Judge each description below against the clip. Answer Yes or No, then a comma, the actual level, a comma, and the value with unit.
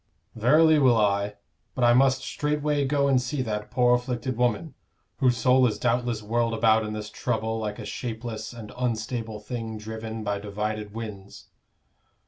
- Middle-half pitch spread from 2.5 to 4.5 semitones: Yes, average, 2.8 semitones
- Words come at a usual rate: Yes, average, 160 wpm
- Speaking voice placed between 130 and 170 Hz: No, low, 115 Hz